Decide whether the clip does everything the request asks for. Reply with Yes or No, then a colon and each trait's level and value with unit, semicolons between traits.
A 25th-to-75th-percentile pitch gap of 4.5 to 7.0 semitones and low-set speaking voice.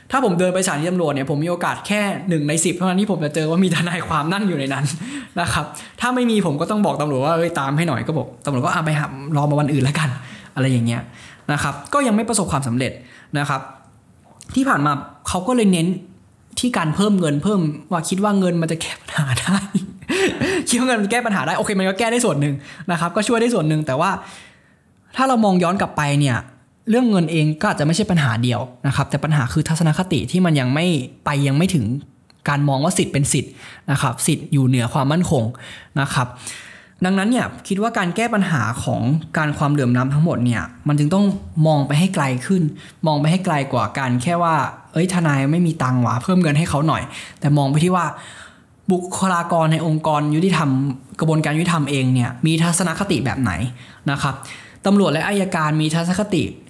No: average, 4.8 semitones; medium, 160 Hz